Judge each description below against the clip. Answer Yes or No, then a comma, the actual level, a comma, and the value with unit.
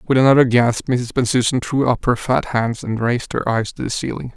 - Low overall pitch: Yes, low, 125 Hz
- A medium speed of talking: No, fast, 235 wpm